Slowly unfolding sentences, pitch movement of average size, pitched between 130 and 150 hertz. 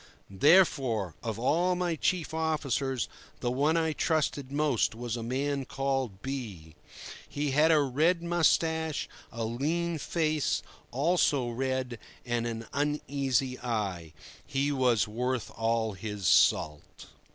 Yes: slow, 125 wpm; average, 4.7 semitones; low, 135 Hz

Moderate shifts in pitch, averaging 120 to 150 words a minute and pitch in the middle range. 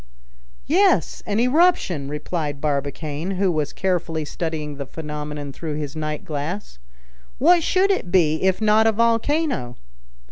No: wide, 6.8 semitones; slow, 135 wpm; medium, 165 Hz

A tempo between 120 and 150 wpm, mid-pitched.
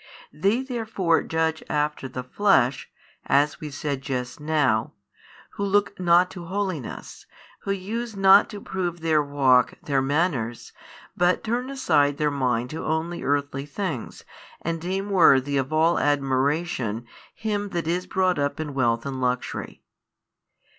Yes: average, 140 wpm; medium, 155 Hz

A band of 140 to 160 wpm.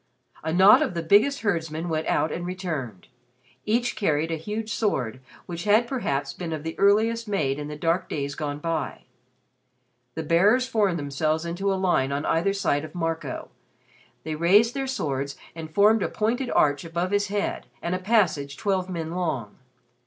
No: average, 175 wpm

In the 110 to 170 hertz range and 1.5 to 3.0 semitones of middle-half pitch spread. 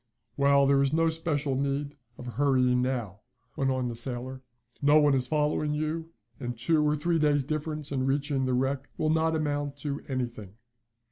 Yes: medium, 140 Hz; narrow, 2.6 semitones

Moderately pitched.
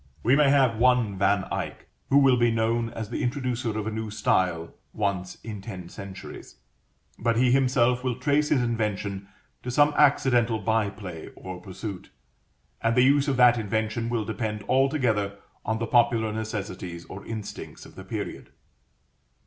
No: low, 115 Hz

